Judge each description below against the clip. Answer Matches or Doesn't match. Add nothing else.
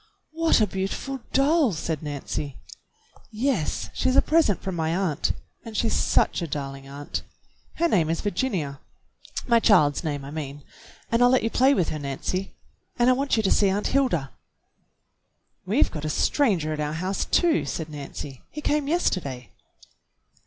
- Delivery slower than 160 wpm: Doesn't match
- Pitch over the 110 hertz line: Matches